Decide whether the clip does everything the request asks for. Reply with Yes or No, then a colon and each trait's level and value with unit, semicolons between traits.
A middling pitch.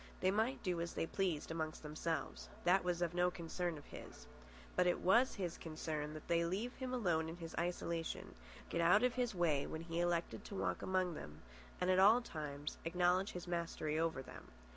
Yes: medium, 175 Hz